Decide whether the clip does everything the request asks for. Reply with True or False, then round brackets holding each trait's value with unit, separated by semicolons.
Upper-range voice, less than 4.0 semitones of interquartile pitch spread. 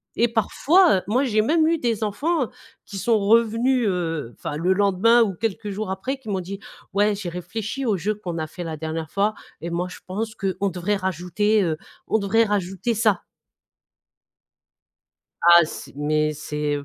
False (200 Hz; 4.3 semitones)